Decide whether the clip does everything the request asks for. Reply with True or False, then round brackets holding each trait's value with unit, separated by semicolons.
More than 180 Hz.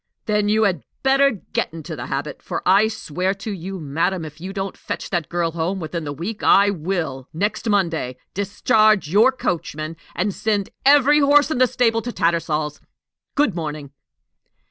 True (190 Hz)